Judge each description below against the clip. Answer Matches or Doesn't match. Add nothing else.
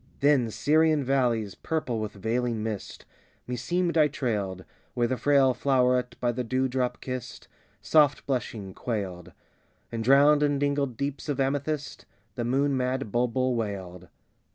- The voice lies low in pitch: Matches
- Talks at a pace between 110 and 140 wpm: Matches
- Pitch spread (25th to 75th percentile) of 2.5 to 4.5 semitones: Matches